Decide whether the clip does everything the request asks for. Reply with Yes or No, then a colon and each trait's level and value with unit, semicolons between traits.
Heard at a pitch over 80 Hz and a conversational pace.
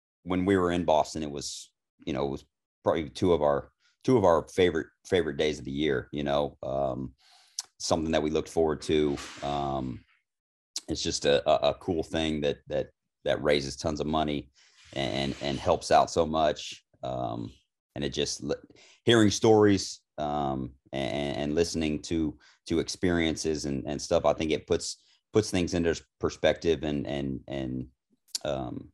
No: very low, 75 Hz; average, 170 wpm